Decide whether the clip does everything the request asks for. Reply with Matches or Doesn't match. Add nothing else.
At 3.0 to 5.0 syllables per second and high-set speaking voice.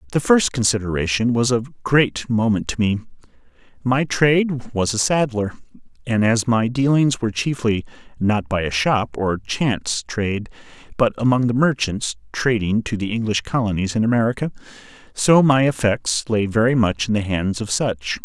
Doesn't match